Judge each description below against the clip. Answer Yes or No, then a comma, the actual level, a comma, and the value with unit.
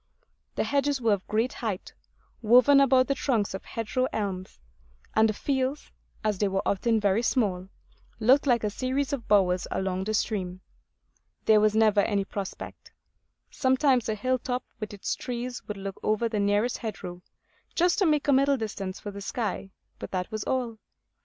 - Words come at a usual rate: Yes, average, 175 wpm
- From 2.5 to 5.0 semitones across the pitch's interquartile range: Yes, average, 4.2 semitones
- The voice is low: No, high, 220 Hz